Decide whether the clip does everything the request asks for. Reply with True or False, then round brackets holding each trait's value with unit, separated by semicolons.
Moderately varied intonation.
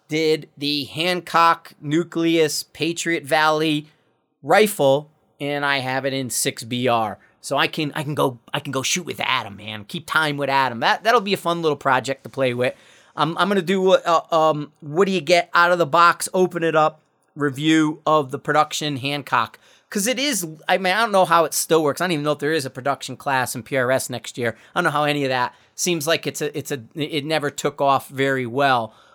True (3.3 semitones)